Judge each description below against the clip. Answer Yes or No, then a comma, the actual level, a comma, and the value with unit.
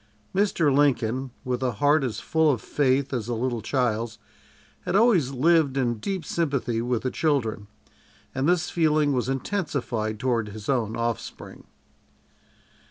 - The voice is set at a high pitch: No, low, 130 Hz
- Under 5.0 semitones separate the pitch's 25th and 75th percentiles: Yes, average, 4.3 semitones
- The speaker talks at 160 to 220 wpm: No, average, 145 wpm